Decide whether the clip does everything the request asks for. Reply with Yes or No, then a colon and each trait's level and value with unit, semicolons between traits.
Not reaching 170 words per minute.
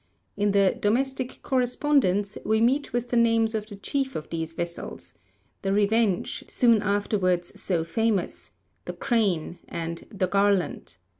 Yes: average, 140 wpm